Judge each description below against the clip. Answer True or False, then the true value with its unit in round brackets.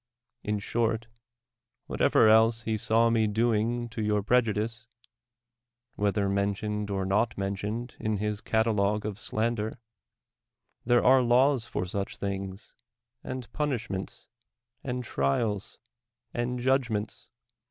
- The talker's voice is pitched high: False (110 Hz)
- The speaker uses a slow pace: True (120 wpm)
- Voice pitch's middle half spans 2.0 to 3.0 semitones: True (2.5 semitones)